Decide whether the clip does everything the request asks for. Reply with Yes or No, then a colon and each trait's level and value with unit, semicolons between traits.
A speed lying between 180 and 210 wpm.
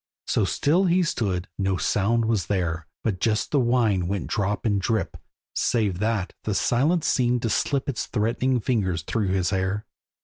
No: average, 170 wpm